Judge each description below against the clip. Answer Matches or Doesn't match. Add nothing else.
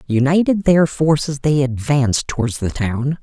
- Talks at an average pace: Matches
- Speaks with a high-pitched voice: Doesn't match